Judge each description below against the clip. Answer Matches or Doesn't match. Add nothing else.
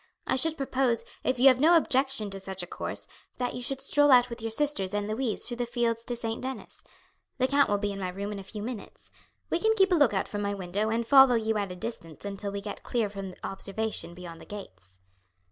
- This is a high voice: Matches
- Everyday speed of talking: Doesn't match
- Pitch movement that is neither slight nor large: Matches